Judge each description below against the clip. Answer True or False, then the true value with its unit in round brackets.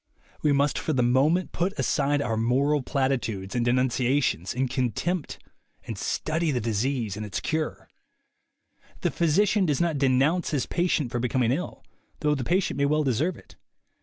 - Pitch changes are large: False (4.2 semitones)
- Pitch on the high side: False (140 Hz)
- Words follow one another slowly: False (165 wpm)